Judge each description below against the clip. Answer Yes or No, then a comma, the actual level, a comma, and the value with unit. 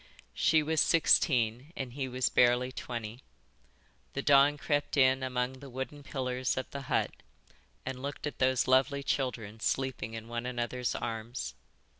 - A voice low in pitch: Yes, low, 130 Hz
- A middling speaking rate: Yes, average, 150 wpm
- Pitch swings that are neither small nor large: No, narrow, 2.3 semitones